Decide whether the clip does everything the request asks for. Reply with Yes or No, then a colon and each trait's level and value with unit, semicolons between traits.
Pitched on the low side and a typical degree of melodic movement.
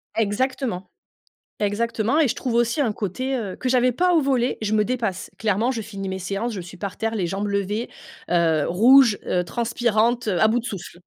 No: high, 220 Hz; average, 3.6 semitones